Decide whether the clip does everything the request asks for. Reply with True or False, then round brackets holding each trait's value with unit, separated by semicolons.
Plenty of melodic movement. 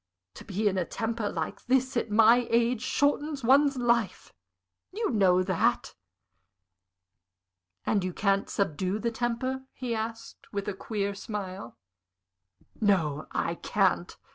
False (3.7 semitones)